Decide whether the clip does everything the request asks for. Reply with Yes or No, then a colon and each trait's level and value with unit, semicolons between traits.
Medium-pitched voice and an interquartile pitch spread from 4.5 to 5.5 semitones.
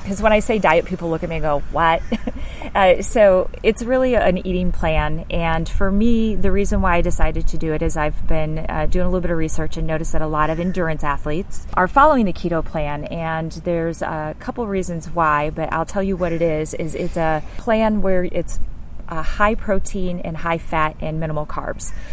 No: medium, 170 Hz; average, 3.6 semitones